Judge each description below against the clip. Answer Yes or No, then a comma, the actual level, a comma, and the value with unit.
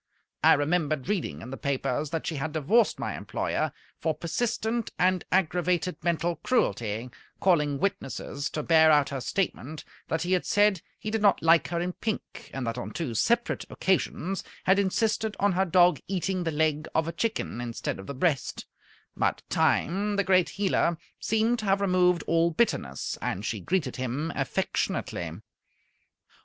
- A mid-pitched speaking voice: Yes, medium, 170 Hz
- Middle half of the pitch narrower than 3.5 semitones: No, average, 4.9 semitones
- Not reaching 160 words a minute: No, average, 165 wpm